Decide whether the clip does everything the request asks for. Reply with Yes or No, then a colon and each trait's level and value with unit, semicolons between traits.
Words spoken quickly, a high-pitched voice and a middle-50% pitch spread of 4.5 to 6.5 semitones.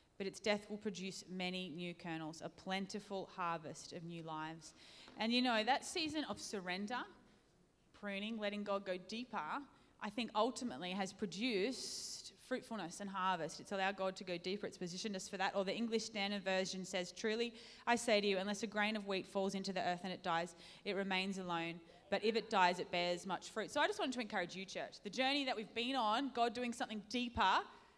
No: fast, 210 wpm; high, 200 Hz; average, 3.5 semitones